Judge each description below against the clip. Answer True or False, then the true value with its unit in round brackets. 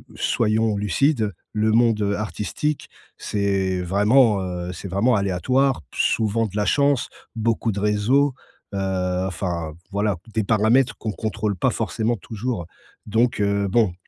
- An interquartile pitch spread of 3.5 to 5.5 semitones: False (2.9 semitones)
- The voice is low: True (105 Hz)